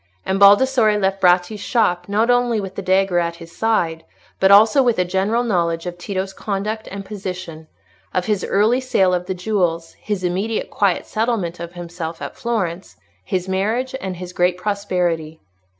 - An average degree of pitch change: Yes, average, 3.3 semitones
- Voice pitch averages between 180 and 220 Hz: Yes, high, 190 Hz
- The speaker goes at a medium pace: Yes, average, 165 wpm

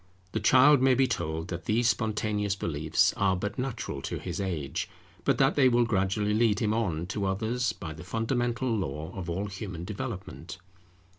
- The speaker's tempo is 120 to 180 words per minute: Yes, average, 175 wpm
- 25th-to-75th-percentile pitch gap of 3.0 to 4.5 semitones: No, average, 5.1 semitones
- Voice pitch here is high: No, low, 105 Hz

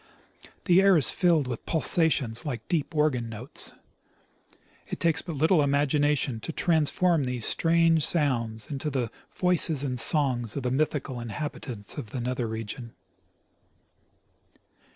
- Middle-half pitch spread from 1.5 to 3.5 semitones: No, average, 4.9 semitones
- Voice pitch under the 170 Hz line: Yes, medium, 140 Hz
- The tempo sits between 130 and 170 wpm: Yes, slow, 135 wpm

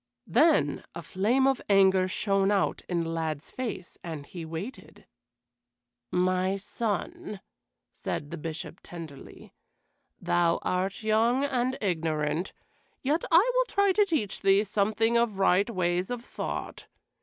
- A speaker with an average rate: No, slow, 130 wpm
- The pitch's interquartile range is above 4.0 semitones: Yes, average, 5.2 semitones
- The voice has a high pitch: Yes, high, 195 Hz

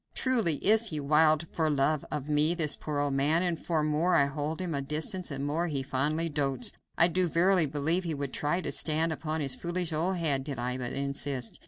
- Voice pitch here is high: No, medium, 155 Hz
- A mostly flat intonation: No, average, 3.2 semitones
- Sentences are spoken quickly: Yes, fast, 225 wpm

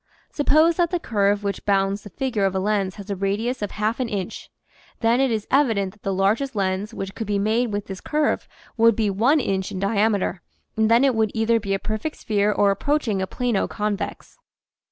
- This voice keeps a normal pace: No, fast, 215 wpm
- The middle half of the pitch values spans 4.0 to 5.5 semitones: No, average, 2.9 semitones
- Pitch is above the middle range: Yes, high, 210 Hz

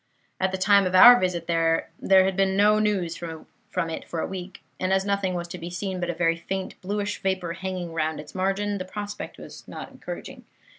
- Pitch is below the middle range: No, medium, 185 Hz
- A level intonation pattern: Yes, narrow, 2.2 semitones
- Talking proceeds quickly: Yes, fast, 210 wpm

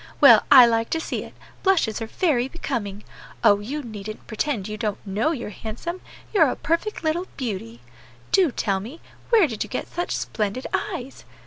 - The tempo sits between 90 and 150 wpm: No, average, 180 wpm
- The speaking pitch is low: No, high, 240 Hz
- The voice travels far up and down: Yes, wide, 7.1 semitones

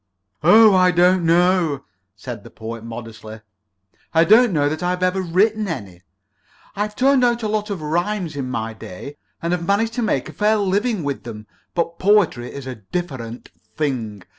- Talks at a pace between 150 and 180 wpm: Yes, average, 175 wpm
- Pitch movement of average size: No, wide, 8.1 semitones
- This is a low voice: No, medium, 175 Hz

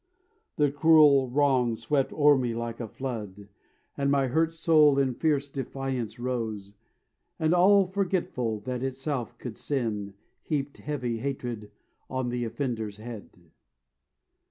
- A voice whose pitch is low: Yes, low, 130 Hz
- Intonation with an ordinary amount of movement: Yes, average, 3.8 semitones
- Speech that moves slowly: Yes, slow, 130 wpm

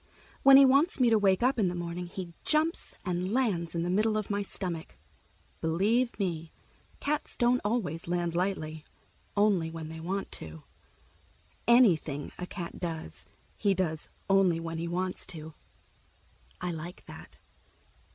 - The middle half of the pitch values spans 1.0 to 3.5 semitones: No, average, 4.3 semitones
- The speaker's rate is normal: Yes, average, 150 wpm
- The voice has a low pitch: No, medium, 180 Hz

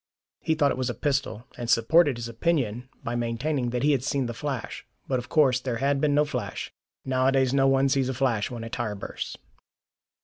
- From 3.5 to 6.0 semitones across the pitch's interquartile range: No, average, 2.9 semitones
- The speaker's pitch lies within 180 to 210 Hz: No, low, 130 Hz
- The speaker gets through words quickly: Yes, fast, 210 wpm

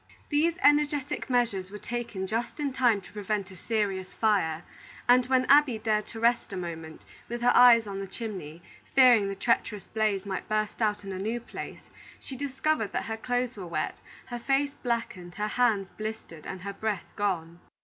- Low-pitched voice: No, high, 220 Hz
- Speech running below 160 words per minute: No, average, 185 wpm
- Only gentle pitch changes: No, average, 3.9 semitones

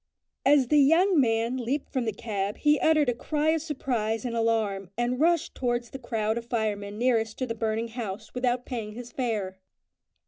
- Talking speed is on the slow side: No, average, 185 wpm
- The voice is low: No, high, 240 Hz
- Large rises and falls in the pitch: No, average, 3.2 semitones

